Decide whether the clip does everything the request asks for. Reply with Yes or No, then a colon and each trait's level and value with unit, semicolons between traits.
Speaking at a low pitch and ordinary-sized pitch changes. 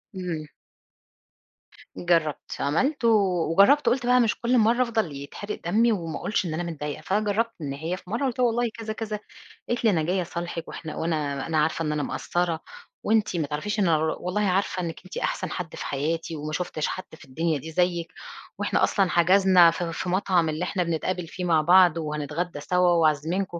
No: medium, 175 Hz; average, 4.2 semitones